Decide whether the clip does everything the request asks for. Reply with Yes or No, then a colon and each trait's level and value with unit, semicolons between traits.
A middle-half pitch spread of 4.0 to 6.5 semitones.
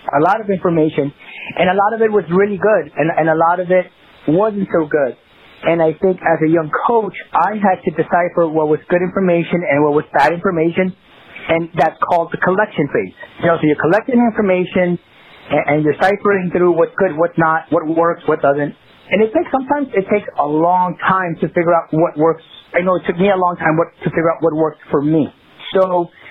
No: average, 2.8 semitones